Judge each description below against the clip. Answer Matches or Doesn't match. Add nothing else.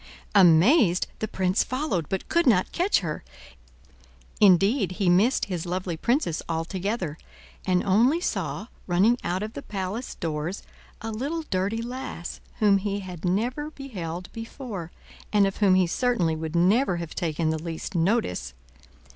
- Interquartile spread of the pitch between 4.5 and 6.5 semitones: Matches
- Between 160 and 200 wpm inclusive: Doesn't match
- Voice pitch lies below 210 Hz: Matches